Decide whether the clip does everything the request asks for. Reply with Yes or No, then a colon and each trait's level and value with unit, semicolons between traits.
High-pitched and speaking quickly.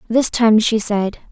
No: high, 220 Hz; average, 185 wpm